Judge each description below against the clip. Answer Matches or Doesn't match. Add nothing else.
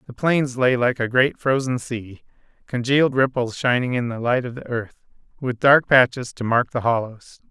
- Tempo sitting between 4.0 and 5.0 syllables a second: Matches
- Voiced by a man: Matches